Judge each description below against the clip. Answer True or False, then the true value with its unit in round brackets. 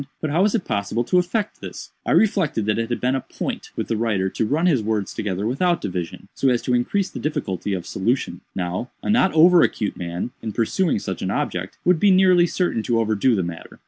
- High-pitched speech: False (120 Hz)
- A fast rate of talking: True (230 wpm)